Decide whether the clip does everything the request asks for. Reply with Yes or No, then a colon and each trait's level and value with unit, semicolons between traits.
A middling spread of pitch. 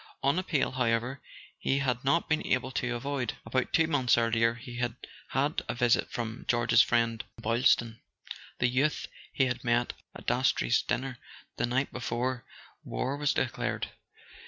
No: narrow, 2.3 semitones